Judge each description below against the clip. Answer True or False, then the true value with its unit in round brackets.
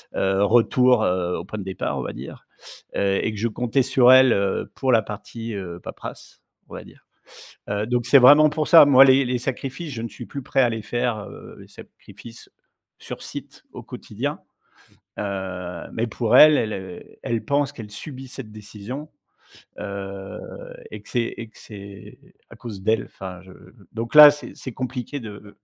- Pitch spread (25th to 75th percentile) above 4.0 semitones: True (4.5 semitones)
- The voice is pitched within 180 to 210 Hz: False (115 Hz)